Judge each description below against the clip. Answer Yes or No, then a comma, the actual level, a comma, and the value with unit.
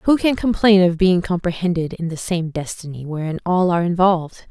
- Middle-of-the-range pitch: Yes, medium, 175 Hz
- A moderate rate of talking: Yes, average, 185 wpm